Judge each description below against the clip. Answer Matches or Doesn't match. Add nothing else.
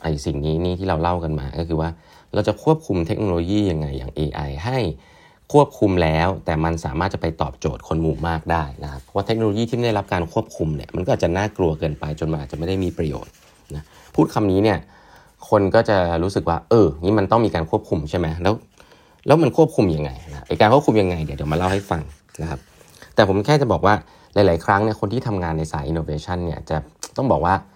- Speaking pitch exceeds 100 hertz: Doesn't match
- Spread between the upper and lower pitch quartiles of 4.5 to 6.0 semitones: Matches